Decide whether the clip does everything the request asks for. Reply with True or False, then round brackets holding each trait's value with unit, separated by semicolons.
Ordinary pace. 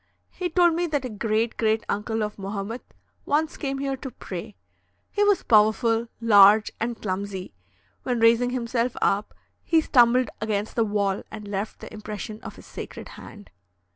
True (165 wpm)